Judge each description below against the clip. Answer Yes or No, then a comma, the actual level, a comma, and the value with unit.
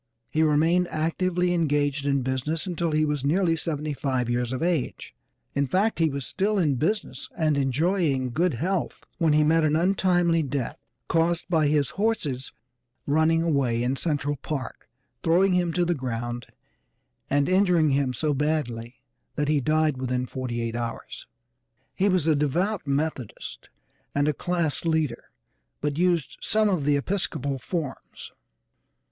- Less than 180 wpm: Yes, average, 150 wpm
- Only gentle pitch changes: No, average, 3.9 semitones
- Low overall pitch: No, medium, 155 Hz